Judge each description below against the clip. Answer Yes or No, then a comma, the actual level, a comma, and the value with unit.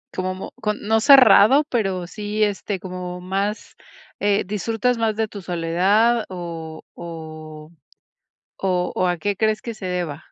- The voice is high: Yes, high, 195 Hz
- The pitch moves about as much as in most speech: Yes, average, 3.5 semitones